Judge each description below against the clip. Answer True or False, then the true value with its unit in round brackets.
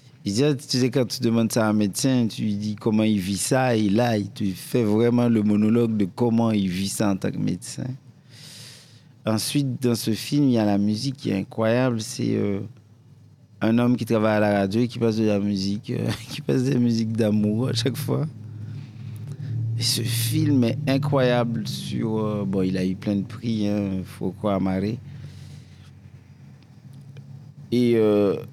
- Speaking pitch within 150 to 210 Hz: False (115 Hz)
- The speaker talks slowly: False (195 wpm)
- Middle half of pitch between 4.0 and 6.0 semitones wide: False (3.4 semitones)